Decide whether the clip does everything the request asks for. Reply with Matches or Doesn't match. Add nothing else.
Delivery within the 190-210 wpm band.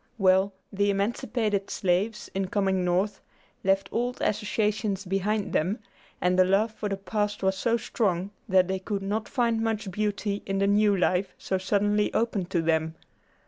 Doesn't match